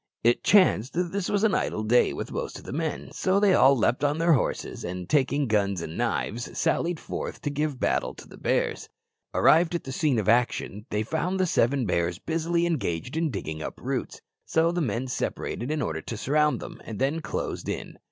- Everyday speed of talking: No, fast, 210 wpm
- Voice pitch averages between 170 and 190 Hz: No, medium, 140 Hz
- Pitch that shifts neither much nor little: No, wide, 7.0 semitones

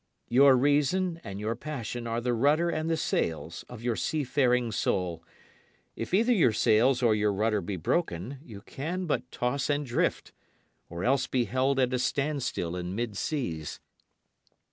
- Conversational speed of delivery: Yes, average, 165 wpm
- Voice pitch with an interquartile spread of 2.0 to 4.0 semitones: No, average, 5.2 semitones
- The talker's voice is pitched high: No, low, 125 Hz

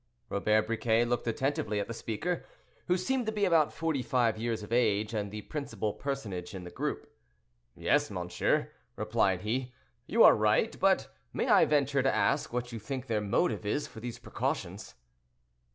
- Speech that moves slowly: No, average, 175 wpm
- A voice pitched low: Yes, low, 115 Hz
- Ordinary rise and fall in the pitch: Yes, average, 4.7 semitones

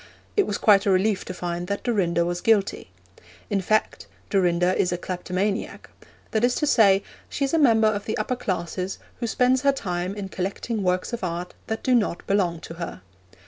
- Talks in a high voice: Yes, high, 195 Hz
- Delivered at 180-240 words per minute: Yes, average, 195 wpm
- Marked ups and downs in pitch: No, average, 3.8 semitones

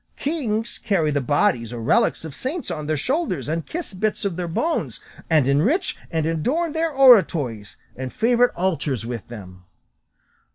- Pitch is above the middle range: No, medium, 165 Hz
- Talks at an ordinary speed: Yes, average, 160 wpm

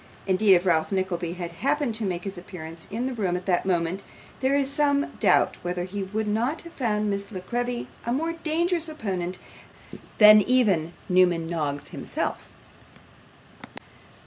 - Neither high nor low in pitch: No, high, 200 Hz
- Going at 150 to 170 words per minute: Yes, average, 160 wpm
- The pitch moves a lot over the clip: Yes, wide, 5.9 semitones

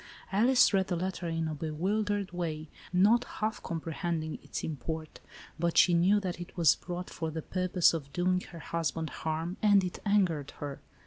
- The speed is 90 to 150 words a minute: No, average, 180 wpm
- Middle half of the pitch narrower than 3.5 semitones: Yes, average, 2.9 semitones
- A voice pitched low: No, medium, 175 Hz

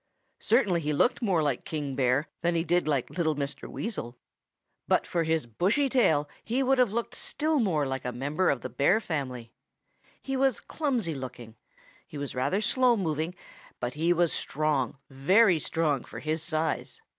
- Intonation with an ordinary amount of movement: No, wide, 6.9 semitones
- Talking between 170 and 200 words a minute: Yes, average, 175 wpm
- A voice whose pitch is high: No, medium, 160 Hz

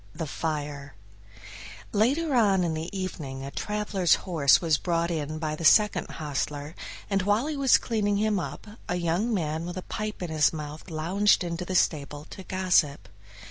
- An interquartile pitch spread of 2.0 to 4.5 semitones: No, average, 5.0 semitones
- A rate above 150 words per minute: Yes, average, 175 wpm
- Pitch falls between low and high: Yes, medium, 175 Hz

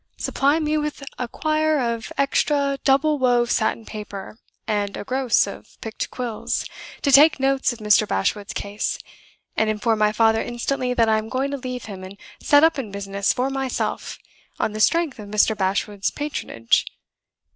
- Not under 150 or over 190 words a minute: Yes, average, 170 wpm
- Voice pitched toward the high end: Yes, high, 240 Hz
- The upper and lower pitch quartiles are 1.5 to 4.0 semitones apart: No, average, 4.5 semitones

